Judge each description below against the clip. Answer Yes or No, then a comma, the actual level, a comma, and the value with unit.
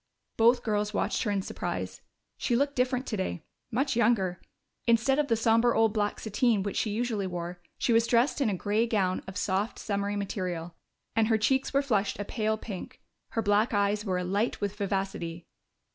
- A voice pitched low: No, high, 210 Hz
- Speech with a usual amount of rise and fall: Yes, average, 3.0 semitones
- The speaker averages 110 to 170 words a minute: No, average, 185 wpm